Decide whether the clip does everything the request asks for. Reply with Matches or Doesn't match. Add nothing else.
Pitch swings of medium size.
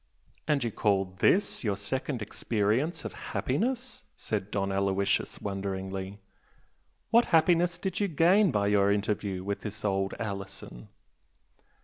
Doesn't match